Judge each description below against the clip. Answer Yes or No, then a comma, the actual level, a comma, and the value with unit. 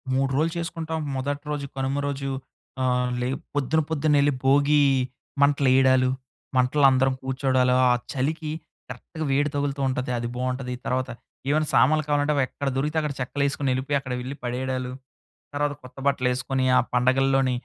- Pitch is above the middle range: No, low, 135 Hz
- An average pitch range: No, narrow, 2.1 semitones